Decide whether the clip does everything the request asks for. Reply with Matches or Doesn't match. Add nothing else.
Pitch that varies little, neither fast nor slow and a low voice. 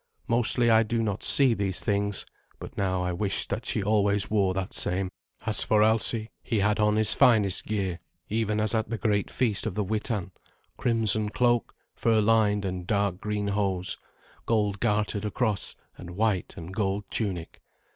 Matches